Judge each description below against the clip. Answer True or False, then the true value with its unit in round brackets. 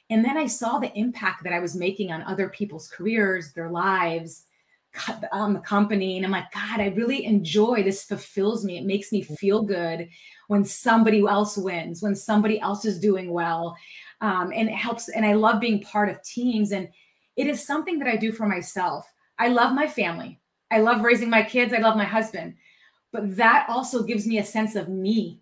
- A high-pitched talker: True (210 Hz)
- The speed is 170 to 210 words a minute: True (205 wpm)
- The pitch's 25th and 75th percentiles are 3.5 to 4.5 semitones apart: False (2.9 semitones)